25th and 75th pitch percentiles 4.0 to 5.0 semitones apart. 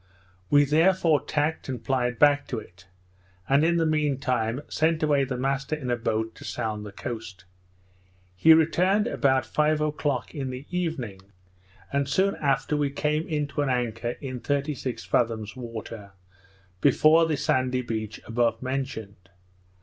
Yes: average, 4.5 semitones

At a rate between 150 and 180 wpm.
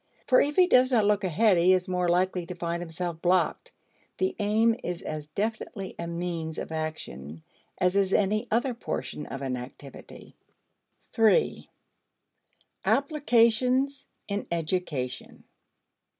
No: slow, 135 wpm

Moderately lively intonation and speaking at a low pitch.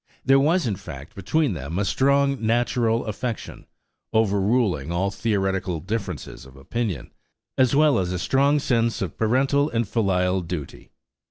No: wide, 5.9 semitones; low, 110 Hz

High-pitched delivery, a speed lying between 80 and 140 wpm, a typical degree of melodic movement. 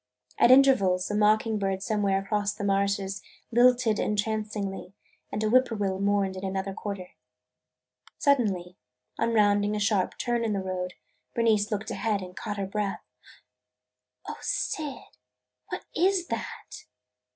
No: high, 205 Hz; slow, 135 wpm; narrow, 2.3 semitones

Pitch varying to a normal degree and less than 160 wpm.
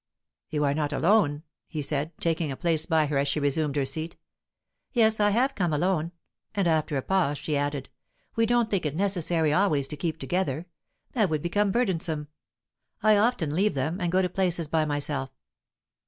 No: average, 4.5 semitones; average, 185 wpm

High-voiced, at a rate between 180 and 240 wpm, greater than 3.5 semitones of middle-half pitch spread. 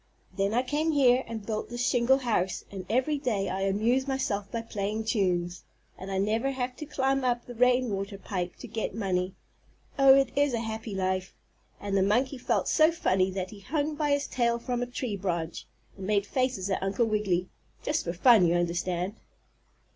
Yes: high, 220 Hz; average, 190 wpm; average, 4.9 semitones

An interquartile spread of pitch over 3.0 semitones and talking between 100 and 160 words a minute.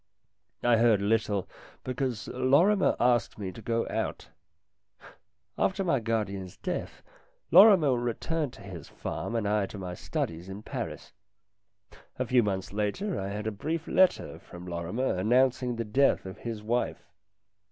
Yes: average, 4.4 semitones; average, 145 wpm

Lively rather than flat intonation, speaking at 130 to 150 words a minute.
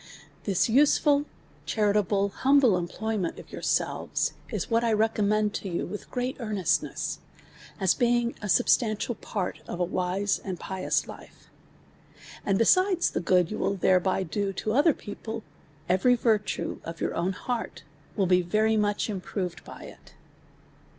No: average, 3.5 semitones; average, 145 wpm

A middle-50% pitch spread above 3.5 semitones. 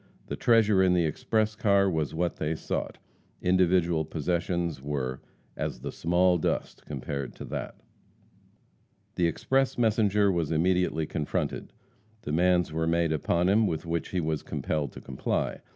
No: average, 3.0 semitones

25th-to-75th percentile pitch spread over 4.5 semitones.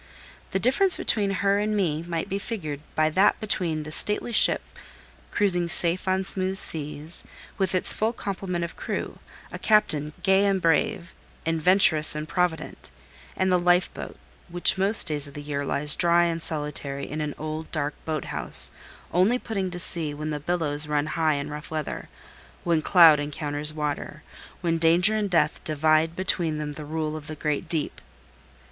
No: average, 3.7 semitones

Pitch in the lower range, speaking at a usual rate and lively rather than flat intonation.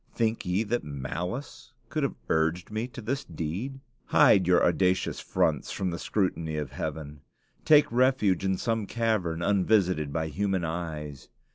Yes: very low, 90 Hz; average, 150 wpm; wide, 5.8 semitones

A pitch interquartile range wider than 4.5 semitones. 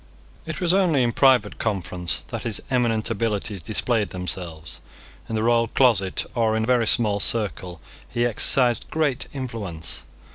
No: average, 3.8 semitones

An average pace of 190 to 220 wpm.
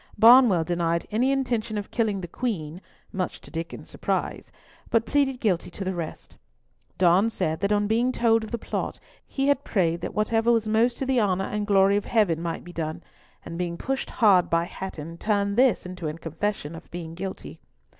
Yes: average, 195 wpm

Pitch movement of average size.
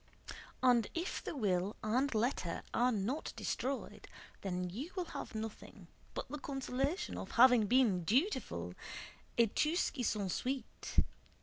Yes: average, 4.7 semitones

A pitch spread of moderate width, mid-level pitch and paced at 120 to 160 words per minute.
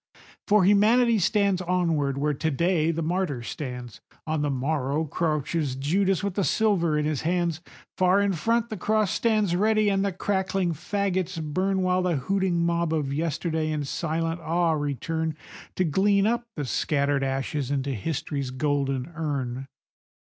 Yes: average, 4.7 semitones; medium, 165 Hz; average, 155 wpm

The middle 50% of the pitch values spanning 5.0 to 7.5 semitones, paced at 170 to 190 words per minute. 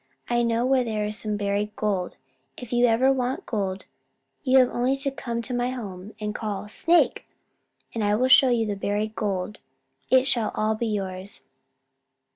No: average, 3.2 semitones; average, 180 wpm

